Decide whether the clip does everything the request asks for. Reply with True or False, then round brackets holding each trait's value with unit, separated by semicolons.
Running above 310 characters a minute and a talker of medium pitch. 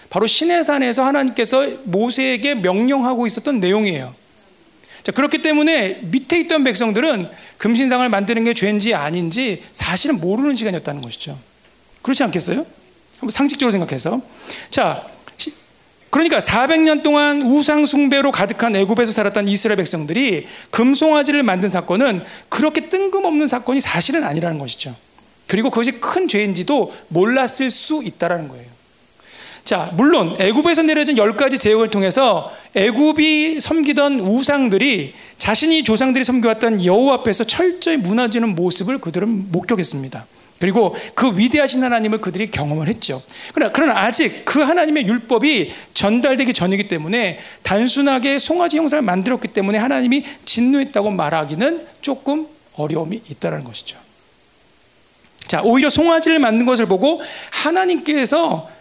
False (350 characters per minute; 250 Hz)